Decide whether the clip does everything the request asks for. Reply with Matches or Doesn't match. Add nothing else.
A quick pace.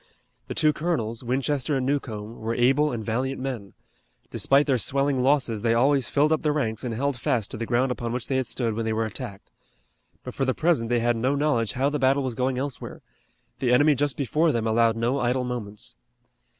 Matches